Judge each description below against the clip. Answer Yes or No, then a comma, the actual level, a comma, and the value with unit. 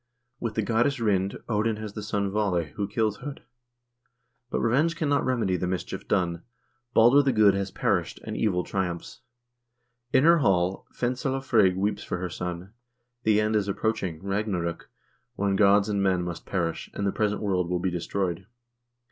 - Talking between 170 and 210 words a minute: Yes, average, 175 wpm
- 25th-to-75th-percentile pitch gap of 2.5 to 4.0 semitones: Yes, average, 3.3 semitones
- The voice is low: Yes, low, 100 Hz